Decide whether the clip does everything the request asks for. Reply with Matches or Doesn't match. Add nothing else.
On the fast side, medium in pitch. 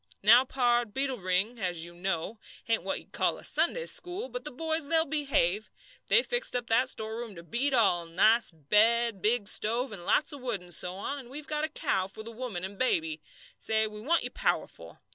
Doesn't match